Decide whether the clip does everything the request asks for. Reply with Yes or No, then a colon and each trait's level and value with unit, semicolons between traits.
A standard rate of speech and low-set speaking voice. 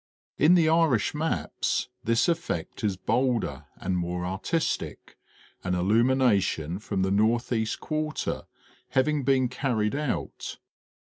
No: slow, 115 wpm; low, 115 Hz